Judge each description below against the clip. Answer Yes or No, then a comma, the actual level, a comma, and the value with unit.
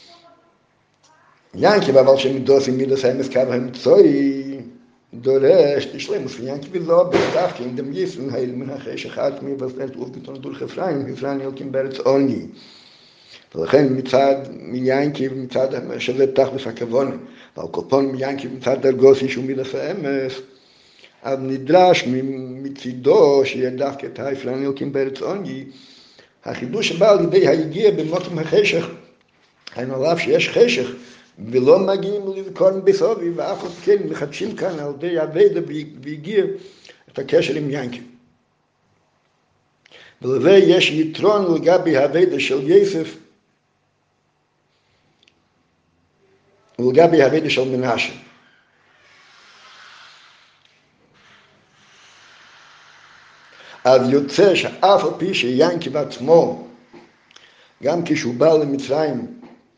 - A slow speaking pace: Yes, slow, 95 wpm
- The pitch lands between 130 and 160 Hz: Yes, low, 135 Hz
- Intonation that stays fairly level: No, wide, 5.5 semitones